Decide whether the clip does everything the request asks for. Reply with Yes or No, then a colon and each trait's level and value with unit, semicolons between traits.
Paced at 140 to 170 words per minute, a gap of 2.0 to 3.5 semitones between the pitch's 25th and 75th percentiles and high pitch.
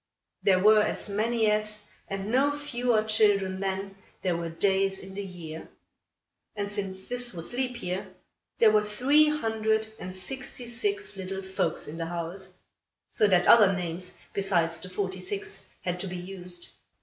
Yes: average, 160 wpm; average, 3.1 semitones; high, 195 Hz